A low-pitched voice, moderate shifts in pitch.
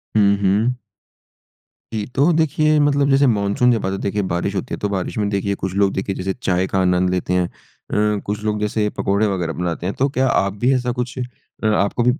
Yes: low, 100 Hz; average, 4.4 semitones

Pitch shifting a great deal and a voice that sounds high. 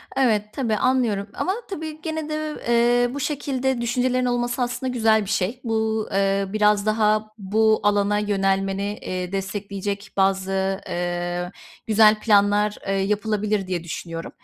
No: average, 3.6 semitones; high, 210 Hz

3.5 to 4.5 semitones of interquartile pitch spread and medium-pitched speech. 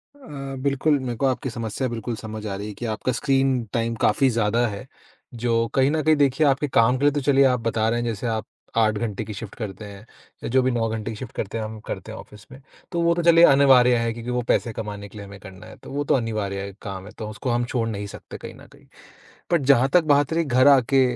No: average, 3.9 semitones; low, 120 Hz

